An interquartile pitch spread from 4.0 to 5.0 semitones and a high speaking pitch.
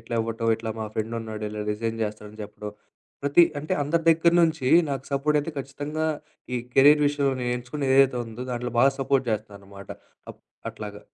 No: average, 4.6 semitones; low, 125 Hz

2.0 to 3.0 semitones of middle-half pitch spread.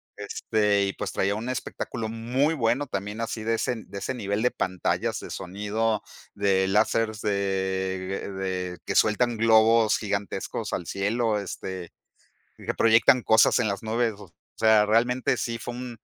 Yes: narrow, 2.5 semitones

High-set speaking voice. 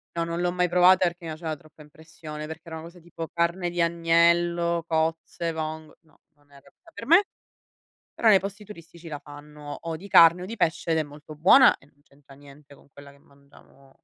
No: medium, 165 Hz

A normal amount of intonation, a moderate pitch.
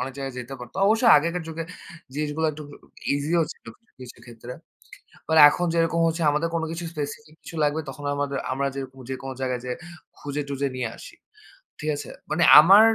Yes: average, 3.3 semitones; medium, 145 Hz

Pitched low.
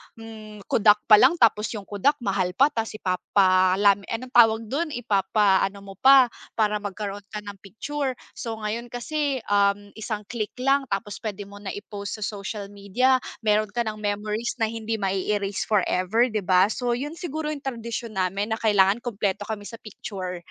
No: high, 210 Hz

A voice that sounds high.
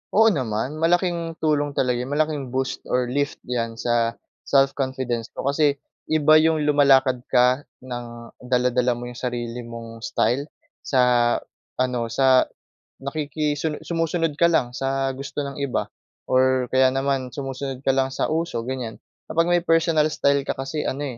No: low, 135 Hz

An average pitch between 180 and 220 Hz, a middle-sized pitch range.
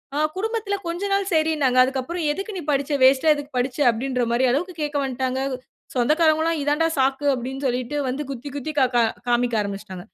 No: very high, 275 Hz; average, 4.0 semitones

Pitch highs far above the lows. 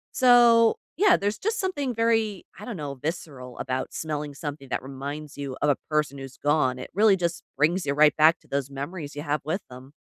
Yes: wide, 6.7 semitones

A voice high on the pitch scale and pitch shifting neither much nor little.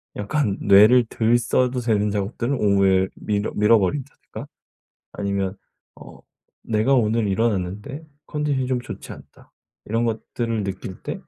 No: low, 110 Hz; average, 3.4 semitones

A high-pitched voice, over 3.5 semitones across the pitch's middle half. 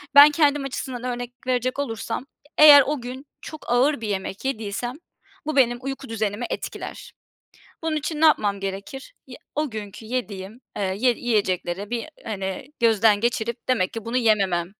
Yes: high, 240 Hz; average, 4.6 semitones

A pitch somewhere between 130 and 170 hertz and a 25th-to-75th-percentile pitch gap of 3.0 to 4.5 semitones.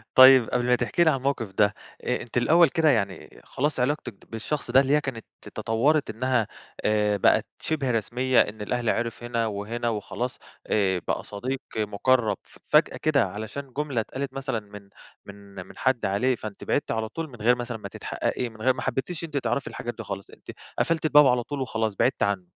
No: low, 120 Hz; average, 3.8 semitones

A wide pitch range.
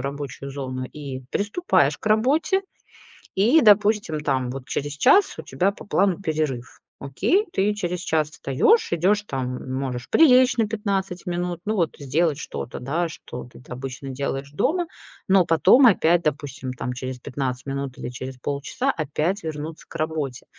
Yes: wide, 6.9 semitones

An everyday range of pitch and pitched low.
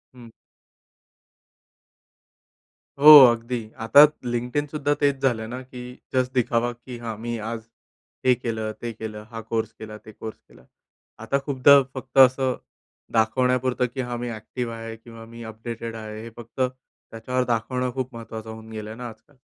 No: narrow, 2.3 semitones; low, 120 Hz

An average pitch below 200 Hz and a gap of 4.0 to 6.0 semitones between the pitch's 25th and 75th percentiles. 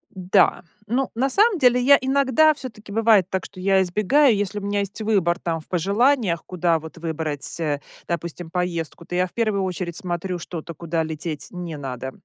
Yes: medium, 185 Hz; average, 4.8 semitones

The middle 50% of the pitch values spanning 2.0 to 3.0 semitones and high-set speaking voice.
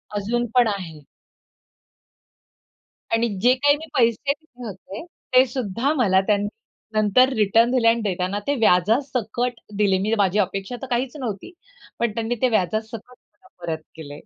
No: average, 4.0 semitones; high, 225 Hz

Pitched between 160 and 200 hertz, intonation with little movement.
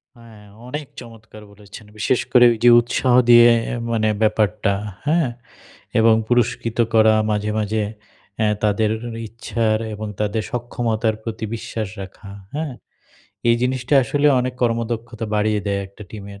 No: low, 110 Hz; narrow, 2.0 semitones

